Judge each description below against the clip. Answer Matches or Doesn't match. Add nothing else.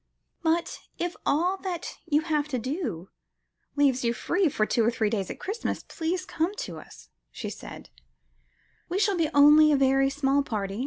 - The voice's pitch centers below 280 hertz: Doesn't match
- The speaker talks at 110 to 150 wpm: Doesn't match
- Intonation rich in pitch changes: Matches